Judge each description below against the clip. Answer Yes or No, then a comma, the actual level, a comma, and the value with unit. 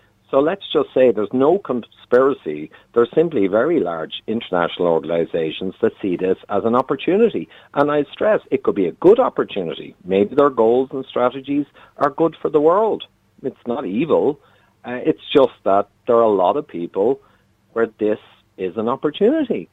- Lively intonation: Yes, wide, 6.1 semitones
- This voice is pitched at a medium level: No, low, 120 Hz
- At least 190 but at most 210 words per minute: No, average, 175 wpm